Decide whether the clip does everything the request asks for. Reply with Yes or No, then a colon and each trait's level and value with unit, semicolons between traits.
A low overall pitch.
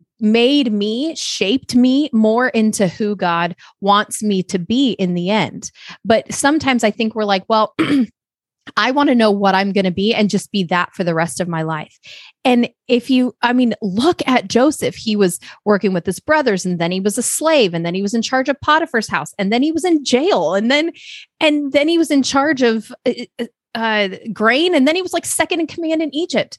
No: high, 230 Hz